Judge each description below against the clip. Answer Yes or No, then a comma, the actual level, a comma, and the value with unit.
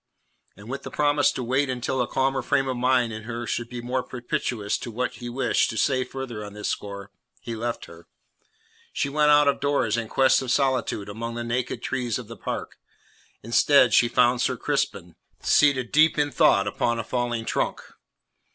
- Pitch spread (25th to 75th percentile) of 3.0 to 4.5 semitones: No, narrow, 2.4 semitones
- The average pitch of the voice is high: No, low, 125 Hz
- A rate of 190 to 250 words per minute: Yes, average, 195 wpm